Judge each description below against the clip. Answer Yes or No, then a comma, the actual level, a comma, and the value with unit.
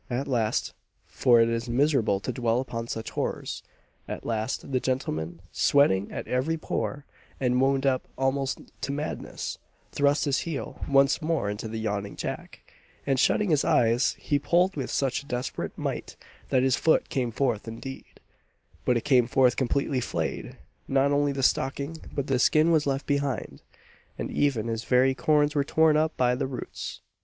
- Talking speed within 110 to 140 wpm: No, average, 170 wpm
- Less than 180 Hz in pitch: Yes, low, 135 Hz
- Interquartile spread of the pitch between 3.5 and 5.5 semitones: No, average, 3.1 semitones